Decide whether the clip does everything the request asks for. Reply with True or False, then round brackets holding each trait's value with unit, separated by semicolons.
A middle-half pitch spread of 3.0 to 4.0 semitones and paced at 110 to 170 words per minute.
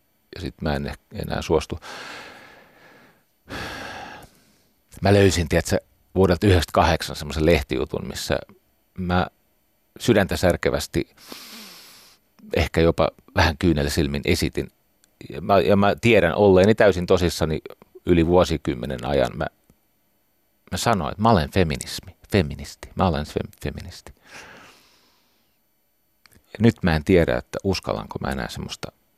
True (3.5 semitones; 115 wpm)